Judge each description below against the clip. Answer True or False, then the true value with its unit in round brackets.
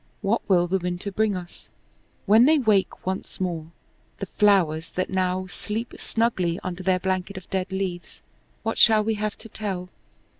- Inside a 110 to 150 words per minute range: False (165 wpm)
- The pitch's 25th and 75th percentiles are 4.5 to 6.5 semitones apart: False (2.8 semitones)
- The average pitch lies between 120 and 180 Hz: False (190 Hz)